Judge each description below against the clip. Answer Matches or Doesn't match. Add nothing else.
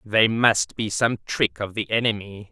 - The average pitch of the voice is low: Matches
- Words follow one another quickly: Doesn't match